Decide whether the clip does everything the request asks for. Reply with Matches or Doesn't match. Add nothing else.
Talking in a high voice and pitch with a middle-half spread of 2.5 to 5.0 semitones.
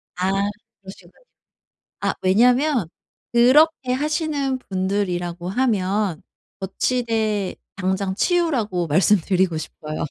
Doesn't match